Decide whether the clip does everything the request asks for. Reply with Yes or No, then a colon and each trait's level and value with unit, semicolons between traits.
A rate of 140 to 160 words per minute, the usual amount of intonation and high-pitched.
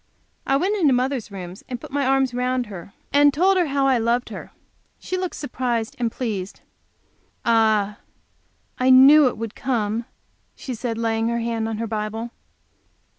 No: average, 170 wpm; average, 3.3 semitones; high, 240 Hz